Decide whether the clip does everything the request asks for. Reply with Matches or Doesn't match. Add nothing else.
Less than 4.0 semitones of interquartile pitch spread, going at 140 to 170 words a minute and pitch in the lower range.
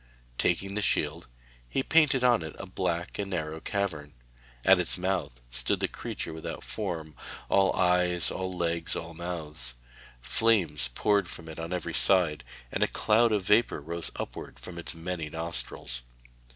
Matches